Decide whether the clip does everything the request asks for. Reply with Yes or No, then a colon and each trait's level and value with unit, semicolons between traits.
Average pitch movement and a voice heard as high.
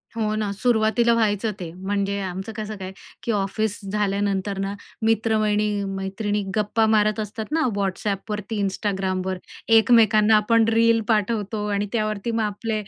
No: narrow, 1.9 semitones; high, 210 Hz